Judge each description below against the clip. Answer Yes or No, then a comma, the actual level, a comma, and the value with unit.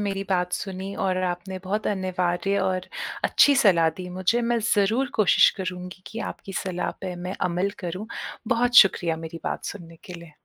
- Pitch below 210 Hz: Yes, medium, 185 Hz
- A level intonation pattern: Yes, narrow, 2.0 semitones